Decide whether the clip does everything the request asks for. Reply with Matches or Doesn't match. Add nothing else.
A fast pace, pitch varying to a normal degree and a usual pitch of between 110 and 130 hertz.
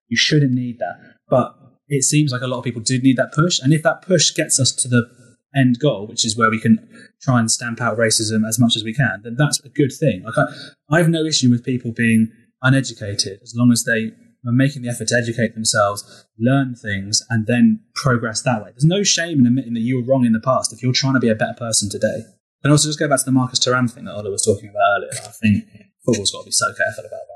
Matches